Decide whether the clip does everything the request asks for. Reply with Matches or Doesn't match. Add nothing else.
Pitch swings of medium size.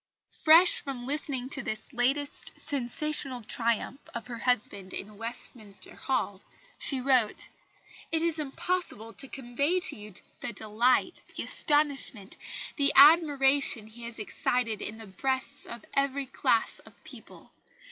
Matches